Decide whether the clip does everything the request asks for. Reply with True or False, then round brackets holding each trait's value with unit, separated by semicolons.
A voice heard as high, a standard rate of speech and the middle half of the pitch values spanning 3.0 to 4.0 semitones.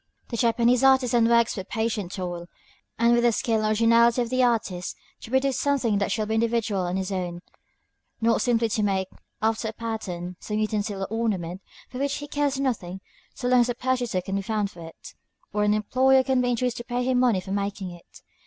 False (225 Hz; 210 wpm; 3.7 semitones)